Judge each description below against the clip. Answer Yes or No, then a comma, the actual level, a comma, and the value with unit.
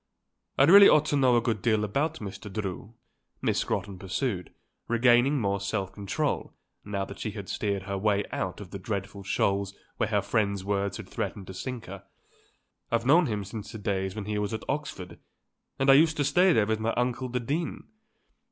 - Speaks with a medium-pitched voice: No, low, 105 Hz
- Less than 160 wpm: No, average, 200 wpm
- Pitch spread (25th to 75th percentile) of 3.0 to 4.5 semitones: Yes, average, 4.0 semitones